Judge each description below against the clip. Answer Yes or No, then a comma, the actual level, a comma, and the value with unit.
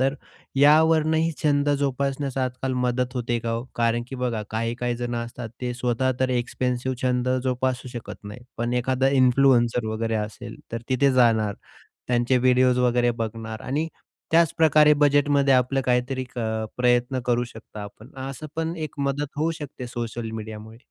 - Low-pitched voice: Yes, low, 125 Hz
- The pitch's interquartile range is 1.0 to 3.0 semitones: Yes, narrow, 2.5 semitones